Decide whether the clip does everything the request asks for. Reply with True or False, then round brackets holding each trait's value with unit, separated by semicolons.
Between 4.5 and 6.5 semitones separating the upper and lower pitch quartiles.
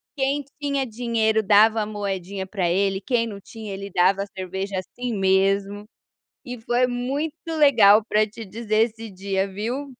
False (3.7 semitones)